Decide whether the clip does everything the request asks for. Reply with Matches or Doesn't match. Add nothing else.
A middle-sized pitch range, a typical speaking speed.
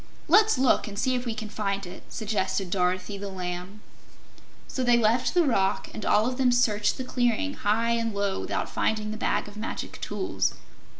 Matches